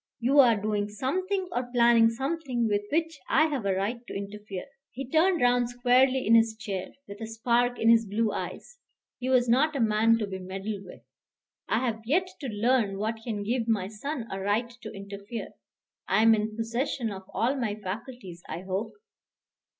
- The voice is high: Yes, high, 230 Hz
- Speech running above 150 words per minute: Yes, average, 190 wpm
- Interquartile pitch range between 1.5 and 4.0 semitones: Yes, average, 3.5 semitones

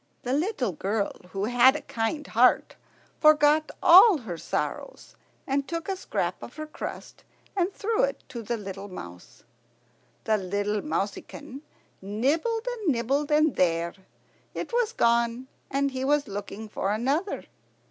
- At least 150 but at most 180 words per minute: No, average, 140 wpm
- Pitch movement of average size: No, wide, 6.3 semitones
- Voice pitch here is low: No, very high, 265 Hz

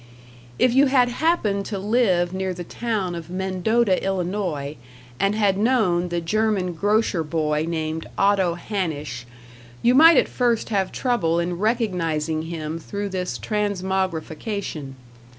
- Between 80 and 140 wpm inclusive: Yes, slow, 135 wpm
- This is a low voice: No, high, 190 Hz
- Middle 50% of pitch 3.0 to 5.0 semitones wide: Yes, average, 4.3 semitones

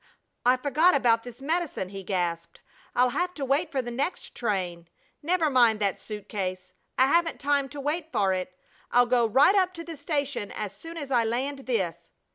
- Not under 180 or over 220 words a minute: Yes, average, 195 wpm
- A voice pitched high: Yes, very high, 250 Hz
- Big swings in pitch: Yes, wide, 6.2 semitones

